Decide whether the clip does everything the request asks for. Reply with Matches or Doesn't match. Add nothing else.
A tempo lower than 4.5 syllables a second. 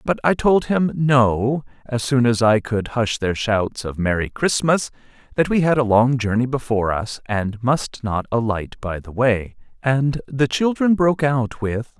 Matches